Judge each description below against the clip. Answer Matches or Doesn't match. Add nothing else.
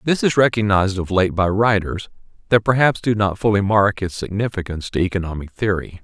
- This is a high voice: Doesn't match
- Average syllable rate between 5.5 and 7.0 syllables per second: Matches